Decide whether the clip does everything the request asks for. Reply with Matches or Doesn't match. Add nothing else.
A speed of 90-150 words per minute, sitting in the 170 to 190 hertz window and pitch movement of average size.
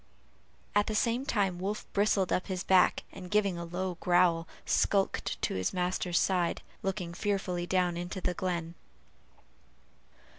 Doesn't match